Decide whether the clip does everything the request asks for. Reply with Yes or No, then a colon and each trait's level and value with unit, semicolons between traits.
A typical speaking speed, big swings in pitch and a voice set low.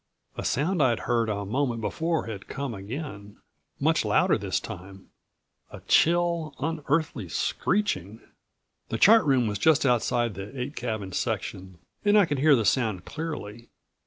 Yes: average, 150 wpm; wide, 6.9 semitones; low, 125 Hz